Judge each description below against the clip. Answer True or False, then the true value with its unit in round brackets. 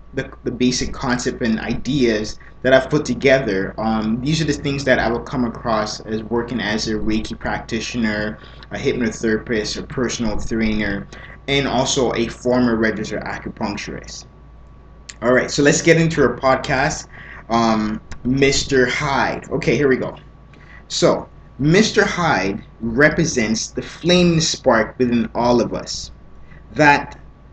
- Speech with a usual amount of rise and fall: True (3.9 semitones)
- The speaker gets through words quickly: False (140 wpm)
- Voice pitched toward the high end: False (125 Hz)